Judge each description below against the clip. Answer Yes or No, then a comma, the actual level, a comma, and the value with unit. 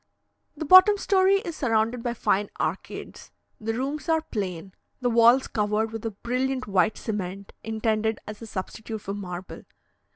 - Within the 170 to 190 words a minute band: No, average, 155 wpm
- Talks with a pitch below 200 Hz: No, high, 225 Hz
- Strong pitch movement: No, average, 4.0 semitones